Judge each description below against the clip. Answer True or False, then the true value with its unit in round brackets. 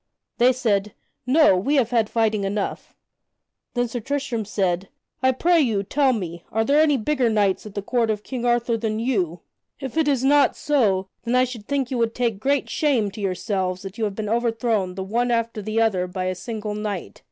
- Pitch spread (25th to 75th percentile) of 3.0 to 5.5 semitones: True (4.1 semitones)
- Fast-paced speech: True (210 wpm)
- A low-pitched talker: False (225 Hz)